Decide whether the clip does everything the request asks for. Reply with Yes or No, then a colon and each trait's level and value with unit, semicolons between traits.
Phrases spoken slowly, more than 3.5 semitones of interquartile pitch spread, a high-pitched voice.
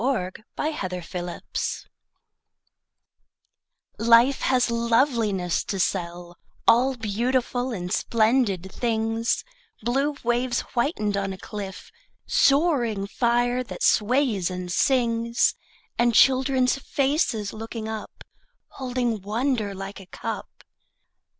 Yes: slow, 100 wpm; average, 4.1 semitones; high, 230 Hz